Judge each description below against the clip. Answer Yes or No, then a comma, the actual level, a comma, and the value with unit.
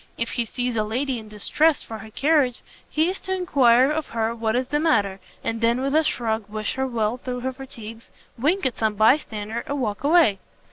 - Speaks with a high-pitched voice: Yes, high, 245 Hz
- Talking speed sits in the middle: No, fast, 220 wpm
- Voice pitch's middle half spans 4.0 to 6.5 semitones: Yes, average, 4.3 semitones